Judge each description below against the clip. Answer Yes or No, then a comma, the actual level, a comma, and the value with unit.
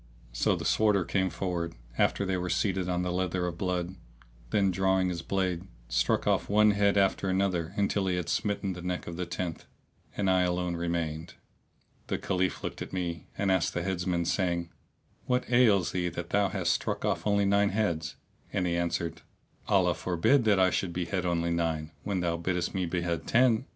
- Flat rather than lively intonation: Yes, narrow, 2.3 semitones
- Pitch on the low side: Yes, very low, 90 Hz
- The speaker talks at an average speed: Yes, average, 190 wpm